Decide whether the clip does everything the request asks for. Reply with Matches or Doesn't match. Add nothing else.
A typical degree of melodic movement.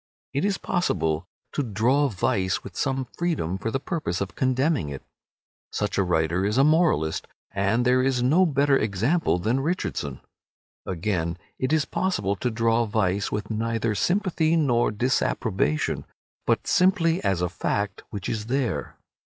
Doesn't match